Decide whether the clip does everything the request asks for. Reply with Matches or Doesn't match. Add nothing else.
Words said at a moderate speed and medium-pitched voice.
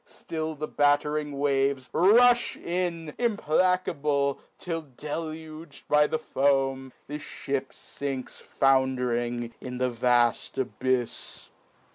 Doesn't match